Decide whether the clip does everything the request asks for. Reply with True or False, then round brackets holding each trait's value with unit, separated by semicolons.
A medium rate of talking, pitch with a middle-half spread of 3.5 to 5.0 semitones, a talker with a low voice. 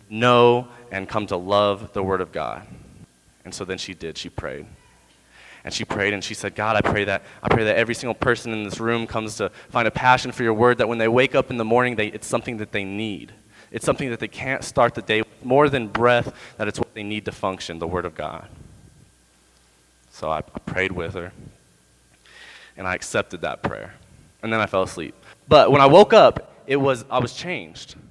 False (225 wpm; 4.2 semitones; 110 Hz)